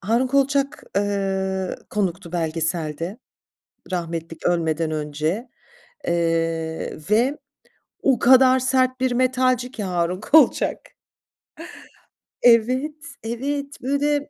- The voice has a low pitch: No, high, 210 Hz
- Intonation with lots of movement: Yes, wide, 7.4 semitones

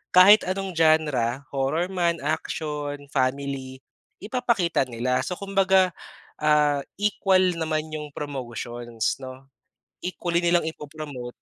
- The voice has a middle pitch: Yes, medium, 150 Hz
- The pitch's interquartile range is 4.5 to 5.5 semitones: Yes, average, 5.0 semitones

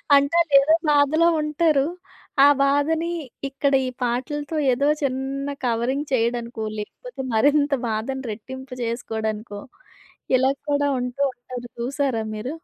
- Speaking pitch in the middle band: No, very high, 265 Hz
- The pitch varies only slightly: No, average, 3.2 semitones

